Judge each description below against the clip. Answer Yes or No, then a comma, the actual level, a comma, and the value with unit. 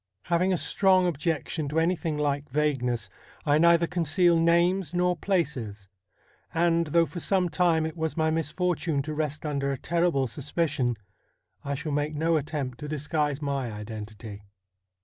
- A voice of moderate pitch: Yes, medium, 155 Hz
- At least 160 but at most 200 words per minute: No, average, 150 wpm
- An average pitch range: Yes, average, 3.3 semitones